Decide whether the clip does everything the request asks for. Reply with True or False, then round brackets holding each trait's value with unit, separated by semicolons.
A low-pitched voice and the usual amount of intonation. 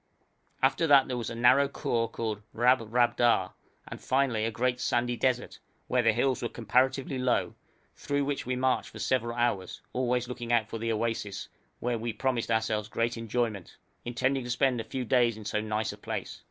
False (120 Hz; 2.1 semitones)